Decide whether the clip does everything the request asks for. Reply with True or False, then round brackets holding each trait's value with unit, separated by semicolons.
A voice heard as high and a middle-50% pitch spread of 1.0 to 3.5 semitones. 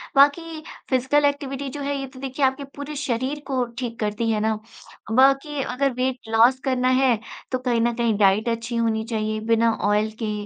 True (255 Hz; 3.2 semitones)